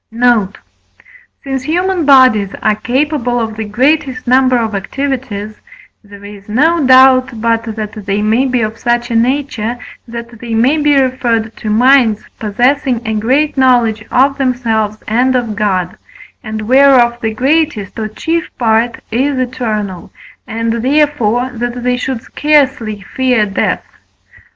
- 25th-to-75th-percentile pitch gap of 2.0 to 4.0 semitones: Yes, average, 3.3 semitones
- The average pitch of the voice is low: No, high, 240 Hz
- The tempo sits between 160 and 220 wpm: No, average, 140 wpm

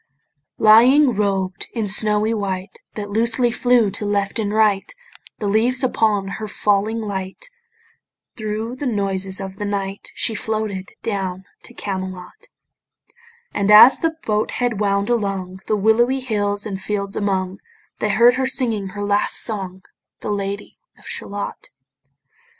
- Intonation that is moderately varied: No, narrow, 2.2 semitones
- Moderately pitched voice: No, high, 205 Hz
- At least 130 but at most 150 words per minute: Yes, average, 140 wpm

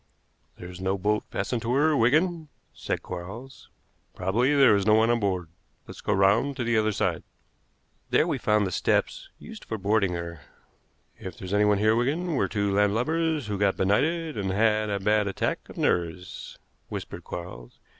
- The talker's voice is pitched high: No, low, 105 Hz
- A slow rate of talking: No, average, 175 wpm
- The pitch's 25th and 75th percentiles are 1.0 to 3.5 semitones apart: No, average, 4.3 semitones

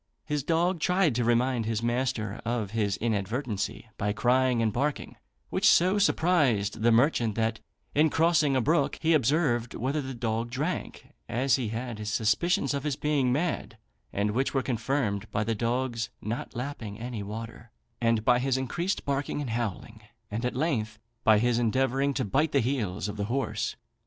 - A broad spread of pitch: No, average, 3.9 semitones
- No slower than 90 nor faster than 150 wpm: No, average, 175 wpm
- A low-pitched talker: Yes, low, 120 Hz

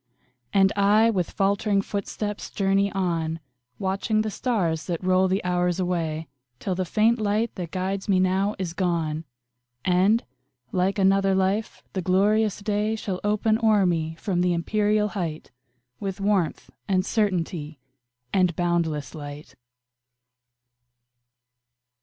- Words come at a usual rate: No, slow, 130 wpm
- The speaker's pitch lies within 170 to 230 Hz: Yes, high, 190 Hz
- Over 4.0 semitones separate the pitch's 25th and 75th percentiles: No, average, 2.8 semitones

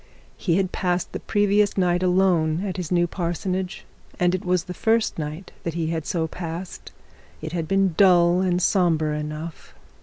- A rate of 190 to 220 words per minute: No, average, 175 wpm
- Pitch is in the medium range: Yes, medium, 180 Hz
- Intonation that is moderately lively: No, narrow, 2.3 semitones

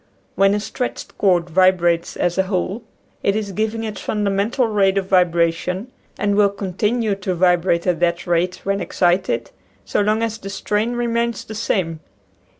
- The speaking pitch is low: No, high, 195 Hz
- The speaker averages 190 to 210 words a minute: No, average, 165 wpm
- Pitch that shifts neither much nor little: Yes, average, 3.2 semitones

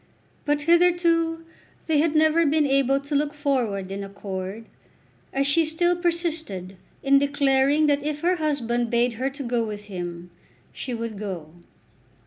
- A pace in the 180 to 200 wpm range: No, average, 150 wpm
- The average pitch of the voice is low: No, very high, 275 Hz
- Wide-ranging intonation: Yes, wide, 5.8 semitones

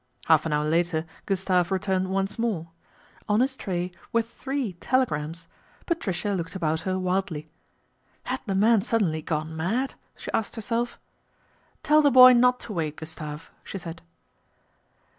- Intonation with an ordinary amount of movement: No, wide, 6.0 semitones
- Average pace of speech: Yes, average, 160 wpm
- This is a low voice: No, high, 190 Hz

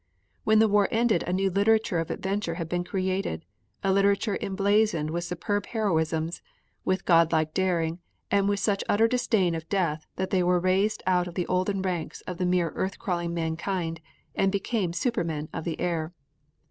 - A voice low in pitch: No, medium, 185 Hz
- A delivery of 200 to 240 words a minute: No, average, 175 wpm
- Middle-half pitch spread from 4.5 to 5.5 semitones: No, average, 3.0 semitones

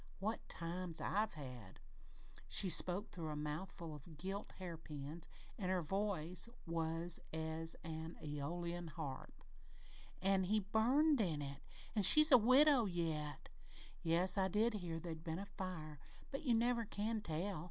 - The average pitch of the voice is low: No, medium, 175 Hz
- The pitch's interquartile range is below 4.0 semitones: No, average, 4.3 semitones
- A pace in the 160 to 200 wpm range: No, average, 145 wpm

